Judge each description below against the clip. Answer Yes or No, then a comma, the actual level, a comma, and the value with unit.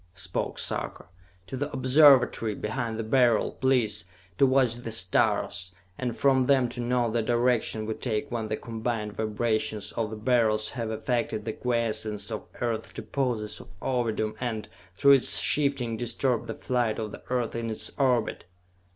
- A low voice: Yes, low, 115 Hz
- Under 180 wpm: Yes, average, 160 wpm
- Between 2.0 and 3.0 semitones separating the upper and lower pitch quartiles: Yes, narrow, 2.5 semitones